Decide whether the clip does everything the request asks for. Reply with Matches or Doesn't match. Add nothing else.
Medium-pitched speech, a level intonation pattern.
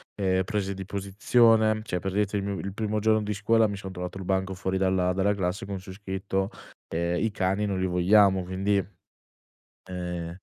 Doesn't match